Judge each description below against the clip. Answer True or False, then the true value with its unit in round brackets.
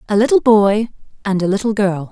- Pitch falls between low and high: False (205 Hz)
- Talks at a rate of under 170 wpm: False (200 wpm)